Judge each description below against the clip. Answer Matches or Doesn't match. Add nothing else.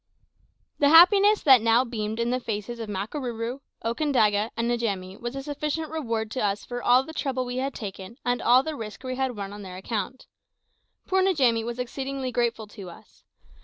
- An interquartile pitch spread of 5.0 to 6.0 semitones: Doesn't match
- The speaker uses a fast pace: Doesn't match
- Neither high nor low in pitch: Doesn't match